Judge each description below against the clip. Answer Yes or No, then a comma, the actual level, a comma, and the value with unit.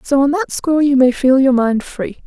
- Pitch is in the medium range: No, very high, 270 Hz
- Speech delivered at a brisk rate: Yes, fast, 265 wpm